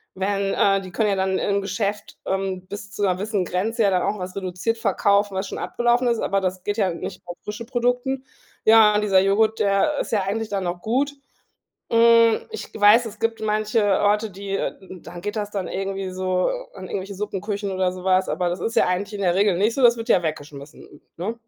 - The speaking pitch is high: Yes, high, 200 Hz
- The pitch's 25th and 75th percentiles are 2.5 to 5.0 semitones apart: Yes, average, 2.9 semitones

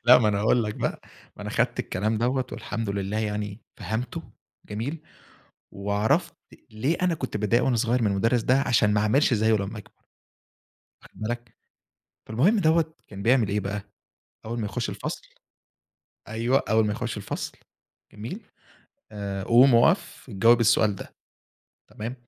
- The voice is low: Yes, low, 110 Hz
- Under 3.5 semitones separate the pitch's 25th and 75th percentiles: Yes, average, 2.9 semitones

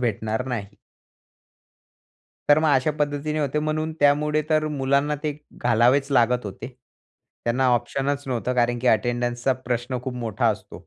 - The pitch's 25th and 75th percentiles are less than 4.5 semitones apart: Yes, average, 3.3 semitones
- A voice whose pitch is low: Yes, low, 130 Hz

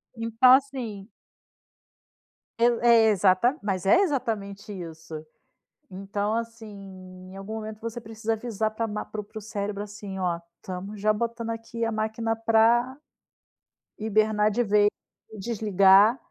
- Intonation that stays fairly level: Yes, narrow, 2.2 semitones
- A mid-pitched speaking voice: No, high, 215 Hz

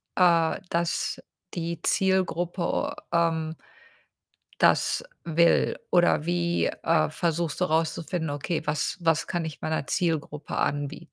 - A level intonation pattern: Yes, narrow, 1.5 semitones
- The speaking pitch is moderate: Yes, medium, 165 Hz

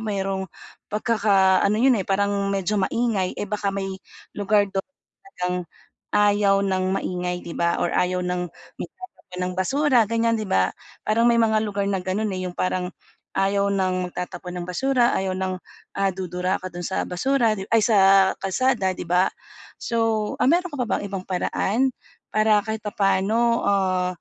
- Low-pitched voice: No, high, 195 Hz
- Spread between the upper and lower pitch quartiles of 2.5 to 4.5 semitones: Yes, average, 2.9 semitones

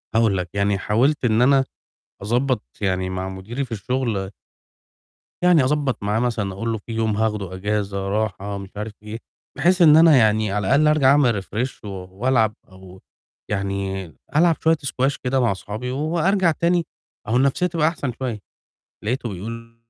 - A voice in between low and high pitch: No, low, 115 Hz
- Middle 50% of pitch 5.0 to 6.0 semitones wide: Yes, wide, 5.4 semitones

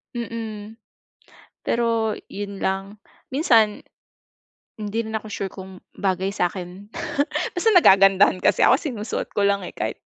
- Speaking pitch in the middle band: No, high, 205 Hz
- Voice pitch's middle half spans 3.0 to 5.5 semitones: No, narrow, 2.6 semitones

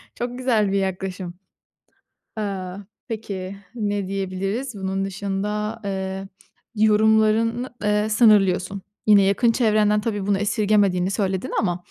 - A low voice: No, high, 205 Hz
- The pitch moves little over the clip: Yes, narrow, 2.0 semitones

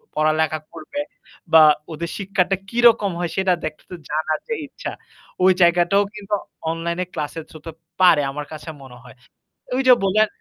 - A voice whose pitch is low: No, medium, 170 Hz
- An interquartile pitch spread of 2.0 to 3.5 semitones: No, average, 4.0 semitones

